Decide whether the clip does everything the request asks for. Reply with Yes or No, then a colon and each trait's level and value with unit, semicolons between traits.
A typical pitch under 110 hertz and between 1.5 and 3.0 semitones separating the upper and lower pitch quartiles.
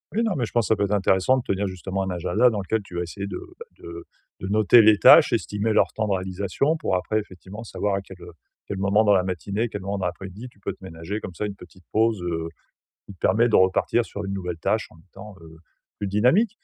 Yes: low, 100 Hz; average, 2.7 semitones